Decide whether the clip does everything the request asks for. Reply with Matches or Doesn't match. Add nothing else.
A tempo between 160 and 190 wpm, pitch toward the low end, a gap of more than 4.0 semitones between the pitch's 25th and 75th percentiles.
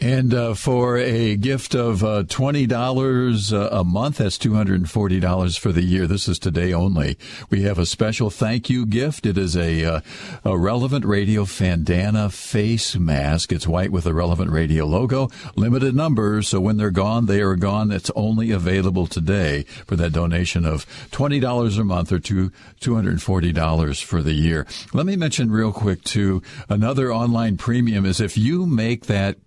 Matches